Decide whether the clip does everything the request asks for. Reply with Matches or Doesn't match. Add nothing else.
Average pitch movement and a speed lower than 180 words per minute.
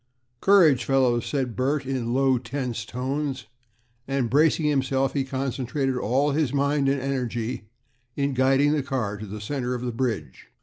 Doesn't match